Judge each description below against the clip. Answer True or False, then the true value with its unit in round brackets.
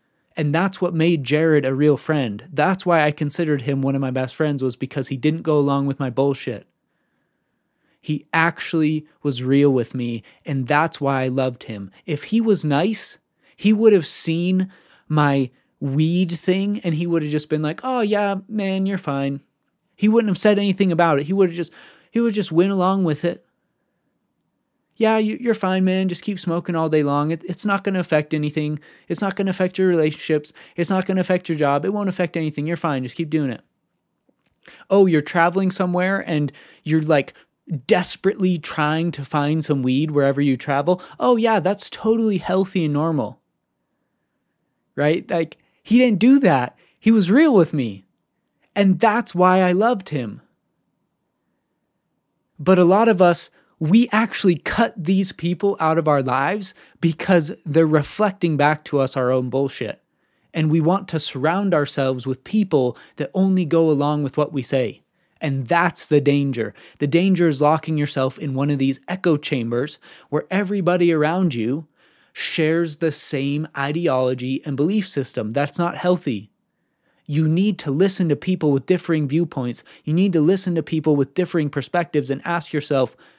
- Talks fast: False (180 wpm)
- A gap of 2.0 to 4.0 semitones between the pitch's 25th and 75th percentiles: False (4.5 semitones)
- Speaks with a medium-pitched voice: True (160 Hz)